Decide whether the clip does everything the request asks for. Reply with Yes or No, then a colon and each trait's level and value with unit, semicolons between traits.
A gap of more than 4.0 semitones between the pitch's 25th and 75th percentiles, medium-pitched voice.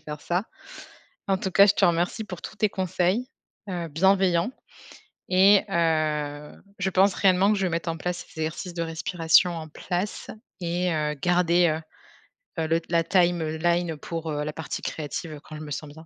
No: narrow, 2.6 semitones; medium, 170 Hz